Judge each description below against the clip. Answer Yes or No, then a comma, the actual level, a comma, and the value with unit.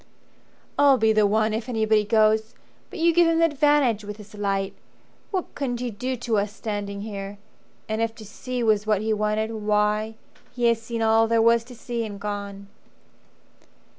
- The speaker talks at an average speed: Yes, average, 185 wpm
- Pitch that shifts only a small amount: Yes, narrow, 2.3 semitones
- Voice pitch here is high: Yes, high, 220 Hz